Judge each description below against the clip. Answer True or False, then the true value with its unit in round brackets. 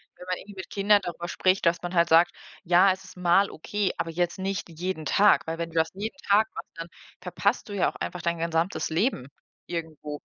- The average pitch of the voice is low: False (175 Hz)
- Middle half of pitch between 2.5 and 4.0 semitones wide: True (2.8 semitones)